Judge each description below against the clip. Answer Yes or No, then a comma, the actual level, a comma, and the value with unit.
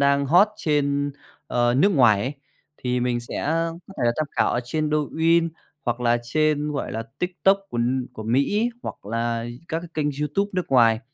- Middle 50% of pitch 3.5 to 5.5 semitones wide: Yes, average, 5.0 semitones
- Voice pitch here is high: No, medium, 140 Hz